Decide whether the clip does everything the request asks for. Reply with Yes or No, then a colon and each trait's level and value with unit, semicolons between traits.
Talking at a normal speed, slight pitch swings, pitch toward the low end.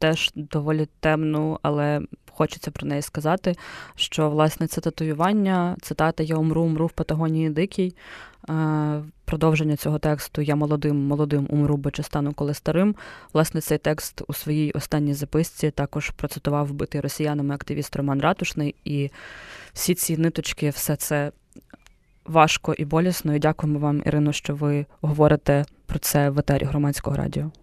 No: average, 145 wpm; narrow, 1.4 semitones; medium, 150 Hz